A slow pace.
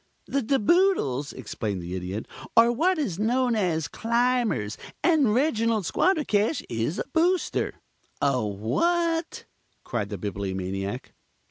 Yes: slow, 120 wpm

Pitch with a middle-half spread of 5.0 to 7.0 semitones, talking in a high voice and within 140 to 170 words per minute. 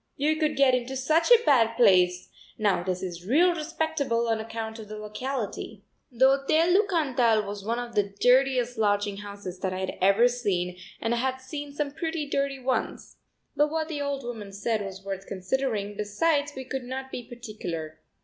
No: average, 5.3 semitones; high, 240 Hz; average, 190 wpm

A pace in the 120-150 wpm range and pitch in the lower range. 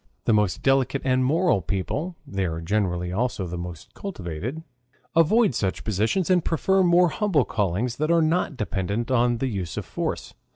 No: average, 170 wpm; low, 120 Hz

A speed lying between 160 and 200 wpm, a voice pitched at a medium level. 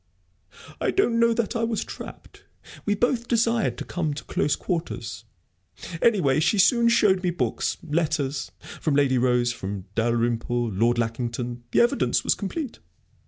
No: average, 150 wpm; medium, 150 Hz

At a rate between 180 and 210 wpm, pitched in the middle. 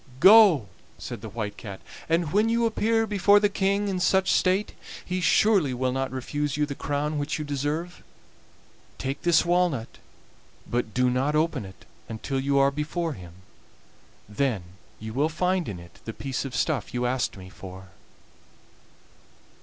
No: average, 160 wpm; medium, 145 Hz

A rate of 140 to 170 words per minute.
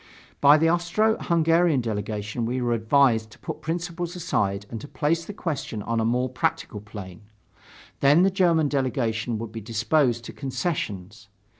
Yes: average, 160 wpm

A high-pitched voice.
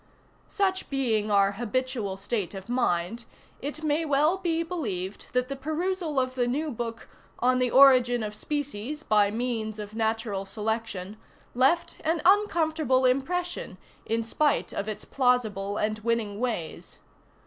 Yes: high, 245 Hz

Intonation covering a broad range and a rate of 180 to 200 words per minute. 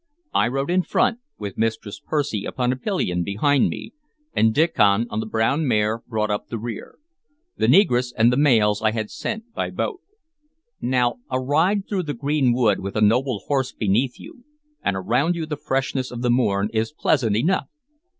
No: average, 5.0 semitones; average, 185 wpm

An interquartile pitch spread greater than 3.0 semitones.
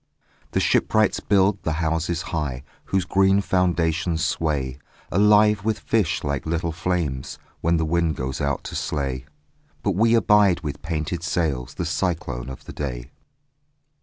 Yes: average, 4.6 semitones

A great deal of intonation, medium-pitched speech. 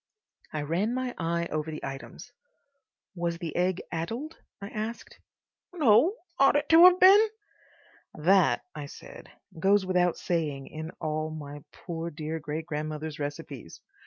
Yes: wide, 5.9 semitones; medium, 170 Hz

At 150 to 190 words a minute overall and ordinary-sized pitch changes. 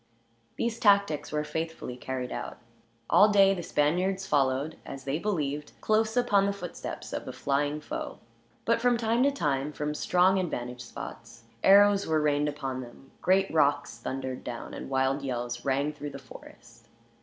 No: average, 165 wpm; wide, 6.4 semitones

